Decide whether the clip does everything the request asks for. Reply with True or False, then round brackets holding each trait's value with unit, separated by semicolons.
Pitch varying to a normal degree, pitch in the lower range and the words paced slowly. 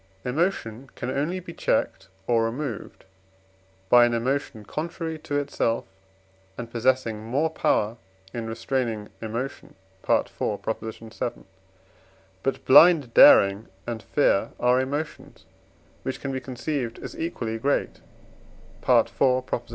True (4.0 semitones; 125 Hz; 110 wpm)